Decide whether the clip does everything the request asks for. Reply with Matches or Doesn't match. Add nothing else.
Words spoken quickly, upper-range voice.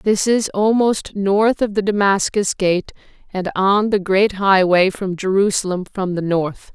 Doesn't match